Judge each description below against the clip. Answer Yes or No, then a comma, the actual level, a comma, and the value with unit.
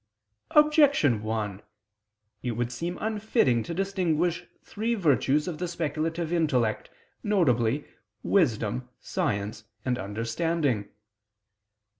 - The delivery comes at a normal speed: No, slow, 95 wpm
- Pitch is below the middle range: No, medium, 150 Hz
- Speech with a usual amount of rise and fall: No, wide, 7.3 semitones